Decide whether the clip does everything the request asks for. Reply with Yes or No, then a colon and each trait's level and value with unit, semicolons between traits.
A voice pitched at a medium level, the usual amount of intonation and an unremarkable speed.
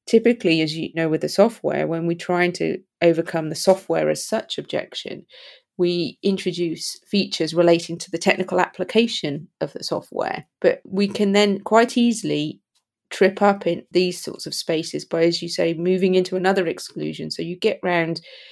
Yes: medium, 180 Hz; average, 3.3 semitones; average, 170 wpm